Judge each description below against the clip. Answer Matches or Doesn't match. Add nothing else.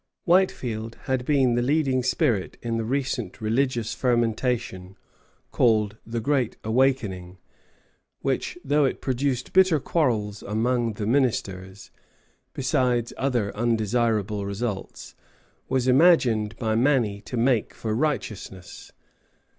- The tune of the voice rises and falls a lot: Doesn't match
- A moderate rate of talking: Doesn't match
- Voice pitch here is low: Matches